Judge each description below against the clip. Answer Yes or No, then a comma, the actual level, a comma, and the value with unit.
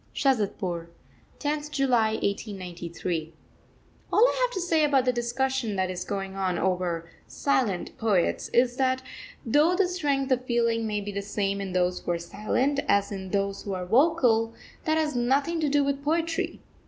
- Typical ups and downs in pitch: No, wide, 6.4 semitones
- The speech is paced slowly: No, average, 170 wpm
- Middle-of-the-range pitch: No, high, 230 Hz